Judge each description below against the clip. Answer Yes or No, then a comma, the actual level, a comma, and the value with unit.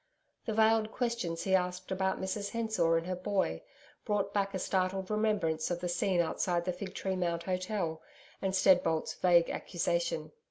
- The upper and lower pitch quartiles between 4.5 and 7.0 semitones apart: No, average, 2.9 semitones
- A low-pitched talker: No, high, 190 Hz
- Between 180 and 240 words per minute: No, average, 165 wpm